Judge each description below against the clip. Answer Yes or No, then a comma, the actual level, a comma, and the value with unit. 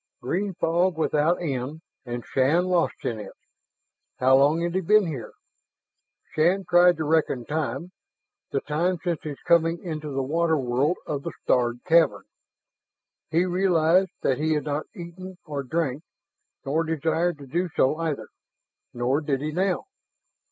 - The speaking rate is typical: Yes, average, 150 wpm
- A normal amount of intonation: Yes, average, 3.8 semitones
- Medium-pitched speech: Yes, medium, 160 Hz